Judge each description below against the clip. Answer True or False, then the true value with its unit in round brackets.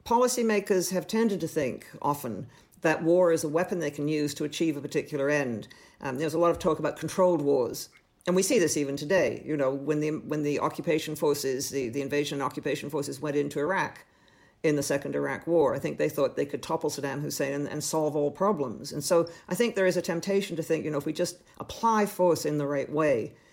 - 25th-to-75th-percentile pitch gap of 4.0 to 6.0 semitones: False (3.4 semitones)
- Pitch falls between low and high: True (155 Hz)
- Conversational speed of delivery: False (230 wpm)